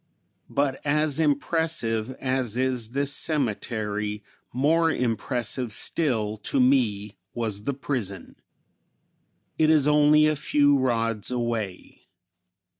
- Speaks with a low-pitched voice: Yes, low, 130 Hz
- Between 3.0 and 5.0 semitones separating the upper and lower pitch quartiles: Yes, average, 4.7 semitones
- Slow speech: Yes, slow, 105 wpm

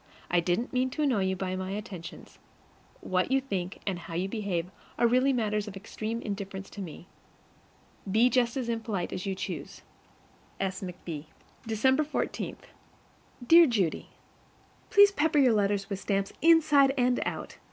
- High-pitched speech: Yes, high, 210 Hz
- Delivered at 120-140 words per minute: No, average, 155 wpm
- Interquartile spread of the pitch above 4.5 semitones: Yes, average, 5.2 semitones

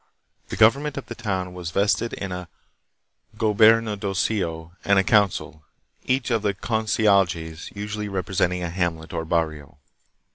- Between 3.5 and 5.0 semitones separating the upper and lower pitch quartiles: Yes, average, 3.9 semitones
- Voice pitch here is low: Yes, low, 100 Hz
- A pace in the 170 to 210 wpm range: No, average, 145 wpm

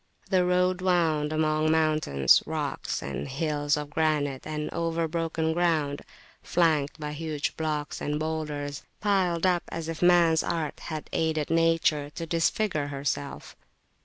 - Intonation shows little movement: Yes, narrow, 2.0 semitones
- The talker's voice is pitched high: No, medium, 155 Hz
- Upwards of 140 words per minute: No, slow, 135 wpm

